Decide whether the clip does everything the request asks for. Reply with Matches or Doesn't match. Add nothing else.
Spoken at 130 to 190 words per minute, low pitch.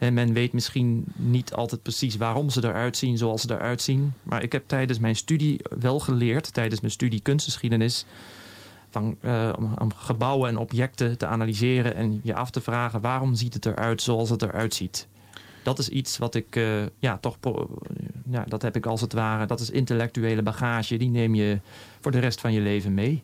Doesn't match